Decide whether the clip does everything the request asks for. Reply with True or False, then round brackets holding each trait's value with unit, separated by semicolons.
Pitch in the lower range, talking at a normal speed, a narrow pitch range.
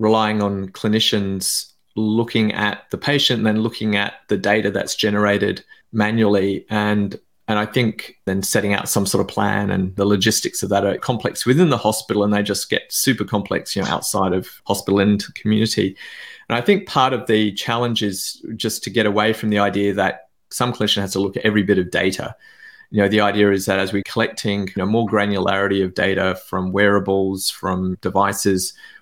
True (105 Hz; 195 wpm; 2.0 semitones)